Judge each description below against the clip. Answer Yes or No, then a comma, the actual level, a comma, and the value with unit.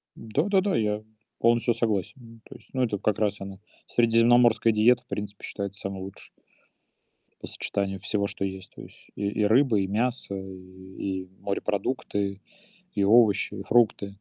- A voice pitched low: Yes, low, 105 Hz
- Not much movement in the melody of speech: No, average, 3.0 semitones